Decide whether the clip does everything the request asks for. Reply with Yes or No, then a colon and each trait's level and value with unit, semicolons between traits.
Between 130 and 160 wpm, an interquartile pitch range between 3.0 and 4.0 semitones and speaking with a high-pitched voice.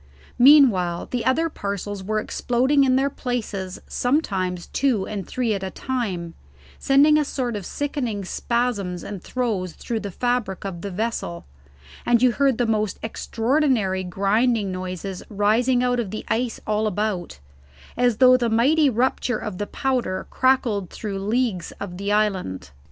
No: average, 155 wpm; average, 4.5 semitones; high, 220 Hz